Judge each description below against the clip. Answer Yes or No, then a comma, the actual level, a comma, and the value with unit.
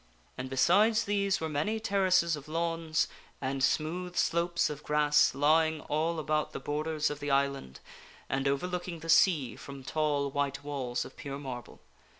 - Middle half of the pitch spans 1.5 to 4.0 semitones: Yes, average, 3.4 semitones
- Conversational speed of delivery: Yes, average, 155 wpm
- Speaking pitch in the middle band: Yes, medium, 155 Hz